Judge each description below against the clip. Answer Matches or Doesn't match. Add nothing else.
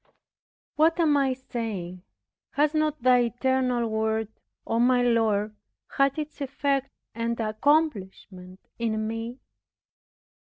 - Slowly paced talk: Matches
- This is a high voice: Matches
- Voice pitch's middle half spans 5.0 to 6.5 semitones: Doesn't match